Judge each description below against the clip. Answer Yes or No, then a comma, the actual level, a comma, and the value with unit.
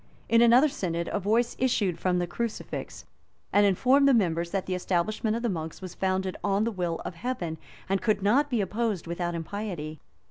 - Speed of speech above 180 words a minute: Yes, average, 190 wpm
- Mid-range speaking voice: No, high, 195 Hz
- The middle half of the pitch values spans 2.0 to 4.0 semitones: No, average, 5.0 semitones